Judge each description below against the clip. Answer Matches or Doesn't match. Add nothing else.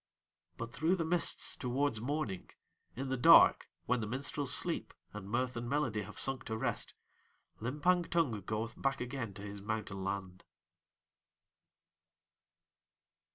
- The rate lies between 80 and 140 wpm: Matches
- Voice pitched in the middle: Doesn't match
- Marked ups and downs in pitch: Doesn't match